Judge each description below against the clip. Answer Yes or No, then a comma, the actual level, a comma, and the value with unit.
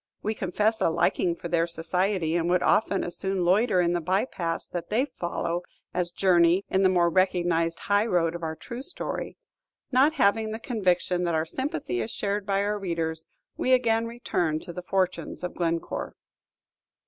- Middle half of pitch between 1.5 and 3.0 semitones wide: No, average, 3.5 semitones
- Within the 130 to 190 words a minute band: Yes, average, 185 wpm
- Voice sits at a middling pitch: Yes, medium, 180 Hz